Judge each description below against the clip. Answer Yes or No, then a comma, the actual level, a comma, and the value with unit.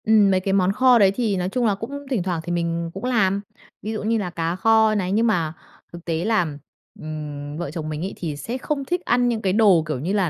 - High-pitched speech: Yes, high, 195 Hz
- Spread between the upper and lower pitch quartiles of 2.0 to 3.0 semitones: No, average, 4.8 semitones